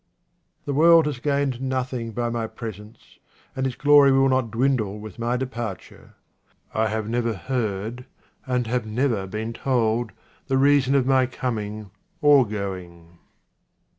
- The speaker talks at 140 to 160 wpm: Yes, average, 145 wpm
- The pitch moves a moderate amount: Yes, average, 3.4 semitones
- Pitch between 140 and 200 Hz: No, low, 120 Hz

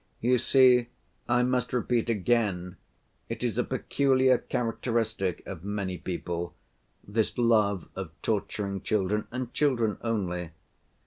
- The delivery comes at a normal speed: No, slow, 120 wpm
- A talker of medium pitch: No, low, 110 Hz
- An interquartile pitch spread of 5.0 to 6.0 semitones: No, average, 4.2 semitones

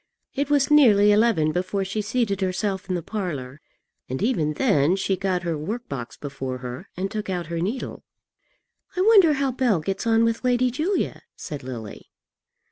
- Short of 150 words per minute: No, average, 175 wpm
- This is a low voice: No, high, 195 Hz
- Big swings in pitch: Yes, wide, 7.4 semitones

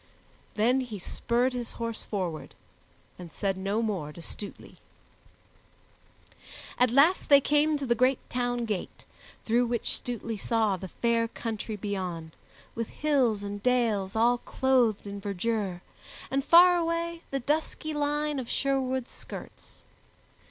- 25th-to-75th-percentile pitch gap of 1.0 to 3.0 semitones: No, average, 4.6 semitones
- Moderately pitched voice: No, high, 235 Hz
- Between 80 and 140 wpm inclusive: Yes, slow, 135 wpm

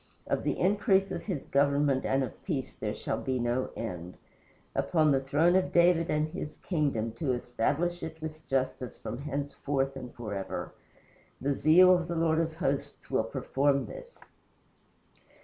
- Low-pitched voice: No, medium, 145 Hz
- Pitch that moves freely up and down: No, average, 4.1 semitones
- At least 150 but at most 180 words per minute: Yes, average, 160 wpm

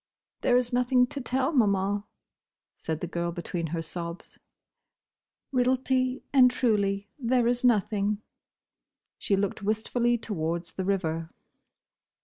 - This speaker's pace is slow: Yes, slow, 120 wpm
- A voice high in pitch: Yes, high, 210 Hz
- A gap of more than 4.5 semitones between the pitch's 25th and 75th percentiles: Yes, wide, 5.5 semitones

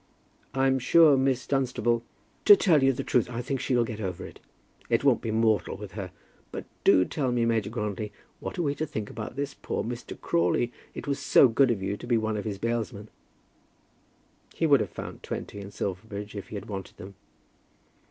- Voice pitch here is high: No, low, 115 Hz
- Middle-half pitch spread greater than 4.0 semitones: Yes, average, 4.4 semitones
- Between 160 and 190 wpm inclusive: No, fast, 205 wpm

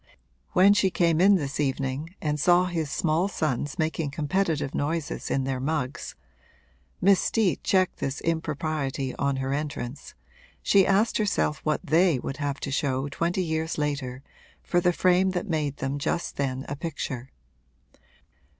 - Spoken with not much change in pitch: No, average, 4.1 semitones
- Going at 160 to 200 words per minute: No, average, 150 wpm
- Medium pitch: Yes, medium, 155 Hz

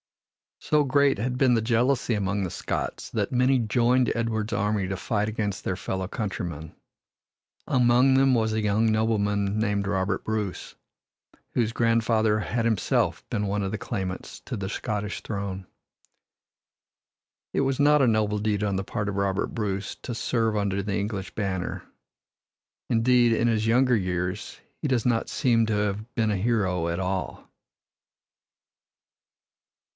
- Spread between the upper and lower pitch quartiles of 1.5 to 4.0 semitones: Yes, average, 2.9 semitones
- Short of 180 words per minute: Yes, average, 150 wpm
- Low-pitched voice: Yes, low, 110 Hz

